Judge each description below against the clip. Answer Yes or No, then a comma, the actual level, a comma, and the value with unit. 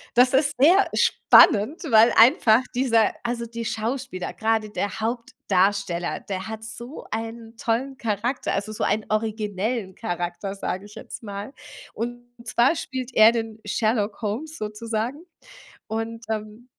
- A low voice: No, high, 225 Hz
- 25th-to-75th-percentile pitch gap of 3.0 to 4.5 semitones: No, narrow, 2.4 semitones